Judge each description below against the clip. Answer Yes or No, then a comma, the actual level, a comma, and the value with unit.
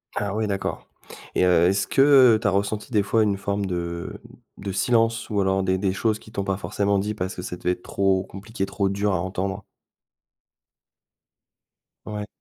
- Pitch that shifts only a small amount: Yes, narrow, 1.9 semitones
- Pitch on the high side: No, low, 100 Hz